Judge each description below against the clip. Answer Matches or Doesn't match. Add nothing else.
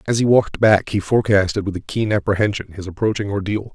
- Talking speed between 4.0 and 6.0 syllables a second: Doesn't match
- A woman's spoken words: Doesn't match